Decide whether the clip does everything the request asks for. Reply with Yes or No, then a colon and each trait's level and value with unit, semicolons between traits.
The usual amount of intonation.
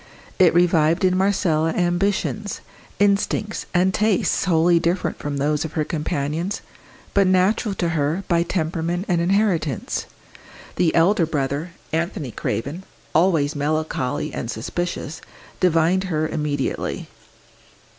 Yes: average, 3.3 semitones